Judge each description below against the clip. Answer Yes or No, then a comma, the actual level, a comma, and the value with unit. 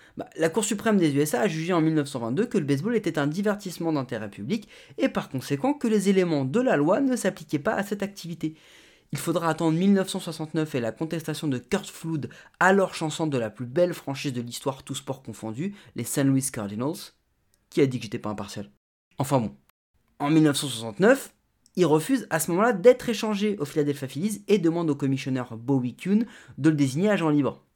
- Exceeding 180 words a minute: Yes, average, 195 wpm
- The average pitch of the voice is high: No, medium, 155 Hz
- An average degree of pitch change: No, wide, 6.6 semitones